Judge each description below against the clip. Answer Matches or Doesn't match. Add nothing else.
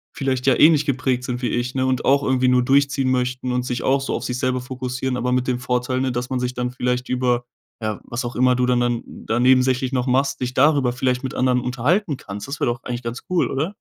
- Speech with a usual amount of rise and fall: Doesn't match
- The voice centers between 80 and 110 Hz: Doesn't match